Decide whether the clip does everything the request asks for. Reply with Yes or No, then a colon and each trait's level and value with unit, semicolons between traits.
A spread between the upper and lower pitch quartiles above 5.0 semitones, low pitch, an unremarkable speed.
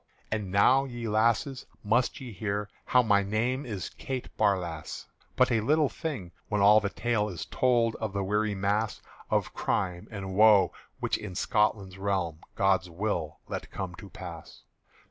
No: average, 3.2 semitones; low, 105 Hz; average, 165 wpm